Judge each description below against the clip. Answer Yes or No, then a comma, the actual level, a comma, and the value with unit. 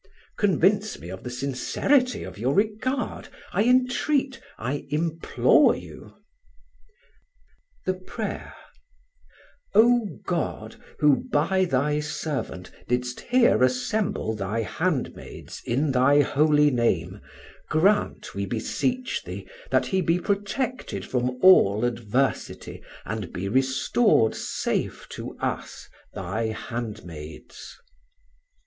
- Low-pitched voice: No, medium, 145 Hz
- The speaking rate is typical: No, slow, 105 wpm